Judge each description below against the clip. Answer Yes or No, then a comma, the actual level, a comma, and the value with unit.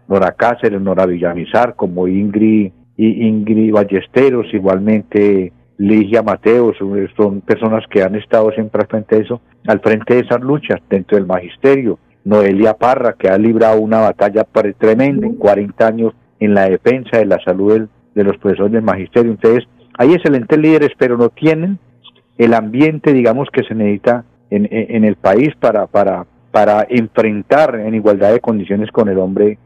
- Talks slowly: No, average, 165 wpm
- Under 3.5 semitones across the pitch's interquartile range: Yes, average, 2.8 semitones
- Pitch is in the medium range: No, low, 110 Hz